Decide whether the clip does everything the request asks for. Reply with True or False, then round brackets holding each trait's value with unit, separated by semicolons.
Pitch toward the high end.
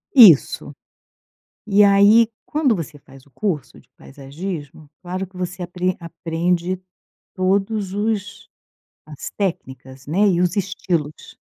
False (180 Hz)